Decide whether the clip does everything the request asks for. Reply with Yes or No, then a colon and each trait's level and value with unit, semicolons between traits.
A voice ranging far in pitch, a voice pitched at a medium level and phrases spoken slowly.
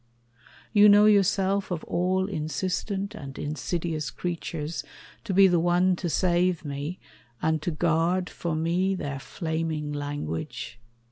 No: average, 3.2 semitones; medium, 175 Hz; slow, 130 wpm